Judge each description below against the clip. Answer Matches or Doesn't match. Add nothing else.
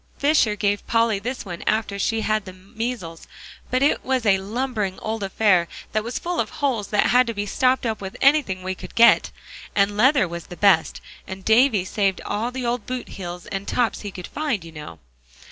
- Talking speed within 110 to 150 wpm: Doesn't match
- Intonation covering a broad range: Doesn't match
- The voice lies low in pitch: Doesn't match